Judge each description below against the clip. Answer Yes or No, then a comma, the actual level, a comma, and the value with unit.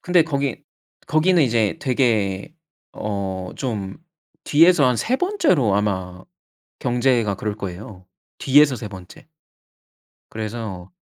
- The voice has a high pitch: No, low, 115 Hz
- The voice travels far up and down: Yes, wide, 6.3 semitones